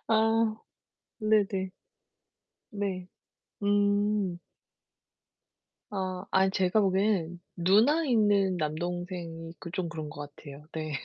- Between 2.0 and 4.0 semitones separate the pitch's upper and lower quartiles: Yes, average, 3.2 semitones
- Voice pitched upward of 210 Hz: No, high, 190 Hz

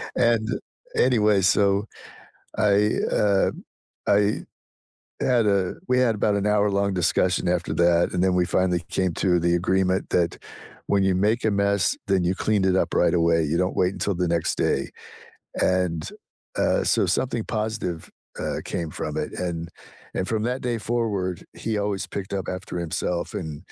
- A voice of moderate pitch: No, very low, 95 Hz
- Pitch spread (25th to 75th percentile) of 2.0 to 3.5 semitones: Yes, average, 2.9 semitones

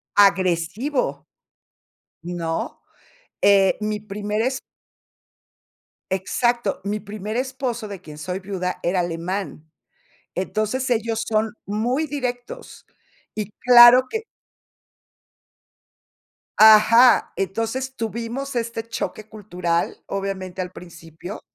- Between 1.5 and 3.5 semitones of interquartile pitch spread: No, average, 4.2 semitones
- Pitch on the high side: Yes, high, 210 Hz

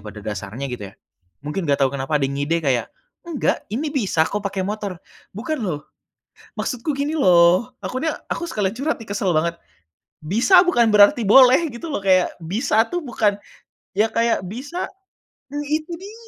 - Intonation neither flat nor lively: No, wide, 8.6 semitones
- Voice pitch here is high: Yes, high, 205 Hz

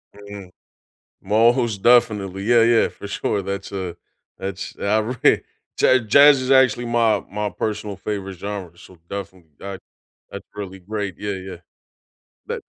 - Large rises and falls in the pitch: No, average, 3.0 semitones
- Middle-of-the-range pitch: No, low, 105 Hz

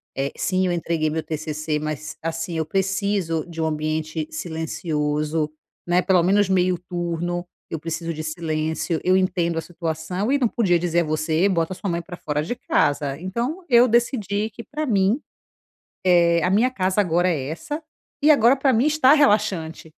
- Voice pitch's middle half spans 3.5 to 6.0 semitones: Yes, average, 4.0 semitones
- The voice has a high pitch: No, medium, 175 Hz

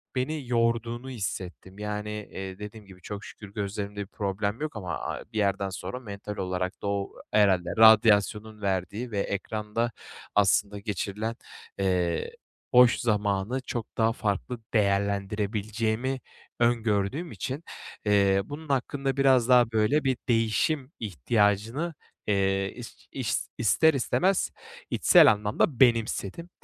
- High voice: No, low, 105 Hz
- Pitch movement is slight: No, average, 3.2 semitones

